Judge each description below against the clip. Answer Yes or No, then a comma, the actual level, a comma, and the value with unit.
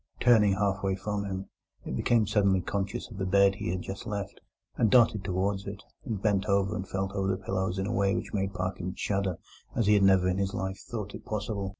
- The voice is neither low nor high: No, low, 100 Hz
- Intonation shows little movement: Yes, narrow, 1.4 semitones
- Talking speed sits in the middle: No, fast, 225 wpm